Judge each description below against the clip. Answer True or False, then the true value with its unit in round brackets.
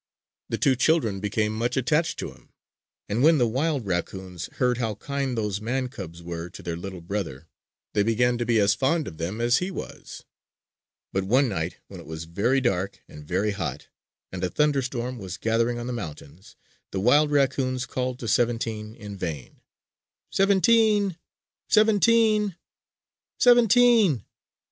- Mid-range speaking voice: False (120 Hz)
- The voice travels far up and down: True (6.3 semitones)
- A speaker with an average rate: True (160 wpm)